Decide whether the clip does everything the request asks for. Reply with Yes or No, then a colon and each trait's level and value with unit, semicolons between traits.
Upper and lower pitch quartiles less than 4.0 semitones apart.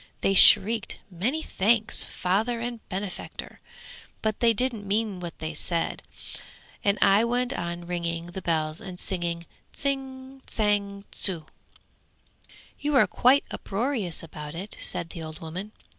No: average, 5.3 semitones